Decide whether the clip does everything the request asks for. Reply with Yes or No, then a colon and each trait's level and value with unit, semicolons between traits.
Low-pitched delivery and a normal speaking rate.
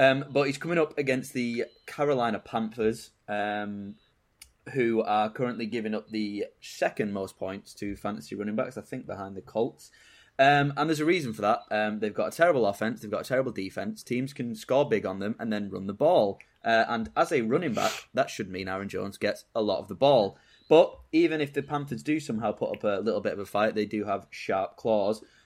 No: low, 115 Hz; fast, 220 wpm